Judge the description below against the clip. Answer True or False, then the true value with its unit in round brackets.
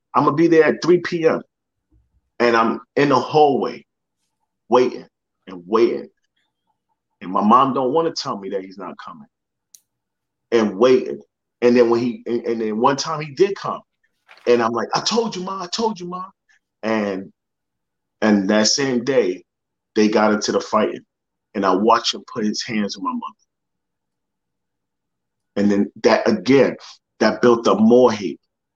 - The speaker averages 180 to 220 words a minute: False (170 wpm)